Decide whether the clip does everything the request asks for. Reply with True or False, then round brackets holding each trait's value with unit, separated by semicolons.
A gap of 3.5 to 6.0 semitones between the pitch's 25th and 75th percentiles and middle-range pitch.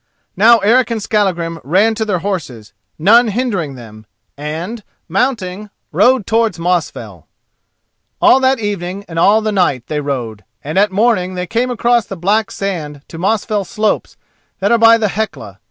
False (5.0 semitones; 200 Hz)